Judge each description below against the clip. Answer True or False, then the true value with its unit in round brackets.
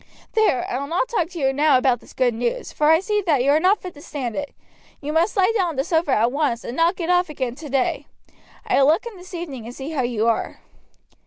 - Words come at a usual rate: False (260 wpm)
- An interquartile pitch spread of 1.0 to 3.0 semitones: False (5.4 semitones)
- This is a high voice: True (300 Hz)